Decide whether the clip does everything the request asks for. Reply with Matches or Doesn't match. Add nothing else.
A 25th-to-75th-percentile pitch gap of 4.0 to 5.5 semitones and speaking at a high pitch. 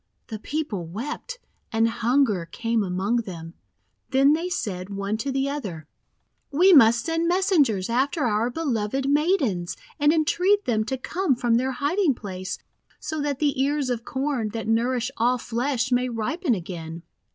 Matches